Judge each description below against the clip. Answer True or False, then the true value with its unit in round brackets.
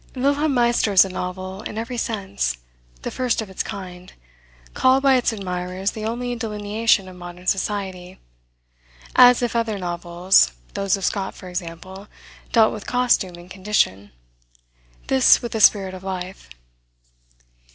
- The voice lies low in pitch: False (195 Hz)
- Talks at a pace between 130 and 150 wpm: True (145 wpm)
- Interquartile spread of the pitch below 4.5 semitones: True (3.9 semitones)